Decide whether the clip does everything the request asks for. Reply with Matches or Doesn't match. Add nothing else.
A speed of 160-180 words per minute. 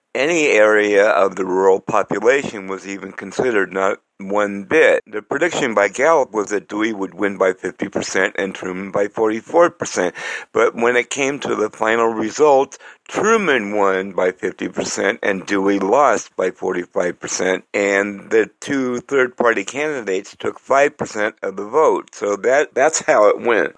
Matches